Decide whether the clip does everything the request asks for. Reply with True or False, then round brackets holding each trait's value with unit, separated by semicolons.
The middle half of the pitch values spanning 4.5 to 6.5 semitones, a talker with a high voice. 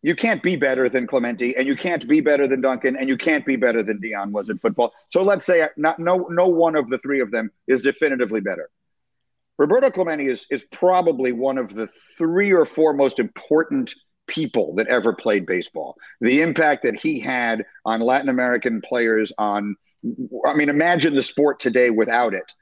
False (5.5 semitones; 140 Hz)